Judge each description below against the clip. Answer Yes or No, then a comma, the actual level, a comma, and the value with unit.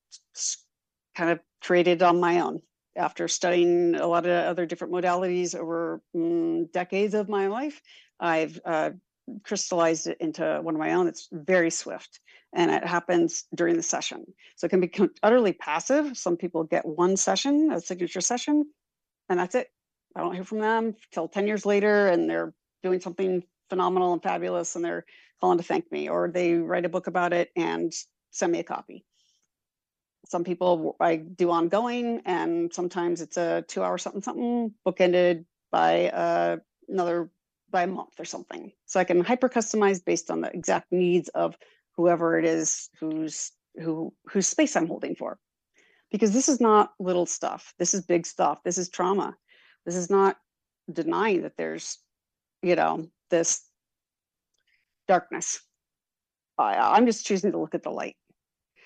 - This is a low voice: No, medium, 180 Hz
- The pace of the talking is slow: No, average, 165 wpm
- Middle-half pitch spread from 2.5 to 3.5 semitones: Yes, average, 2.8 semitones